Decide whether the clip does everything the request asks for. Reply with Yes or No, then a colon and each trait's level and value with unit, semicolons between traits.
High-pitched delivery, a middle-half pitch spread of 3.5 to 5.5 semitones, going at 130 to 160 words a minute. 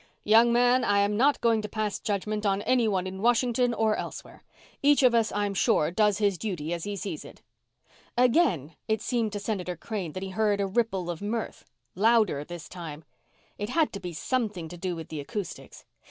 No: high, 205 Hz; average, 4.1 semitones; average, 195 wpm